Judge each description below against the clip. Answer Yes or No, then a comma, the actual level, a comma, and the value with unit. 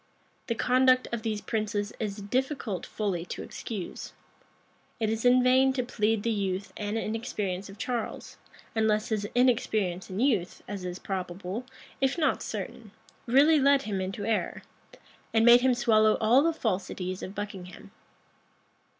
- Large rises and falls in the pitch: No, average, 3.8 semitones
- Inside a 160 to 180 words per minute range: No, average, 150 wpm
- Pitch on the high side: Yes, high, 220 Hz